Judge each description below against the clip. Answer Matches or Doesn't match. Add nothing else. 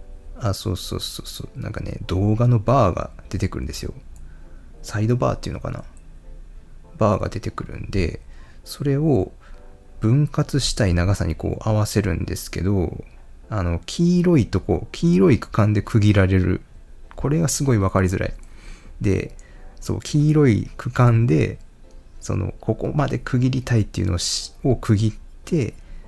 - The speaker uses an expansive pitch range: Matches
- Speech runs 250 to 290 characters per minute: Matches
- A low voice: Matches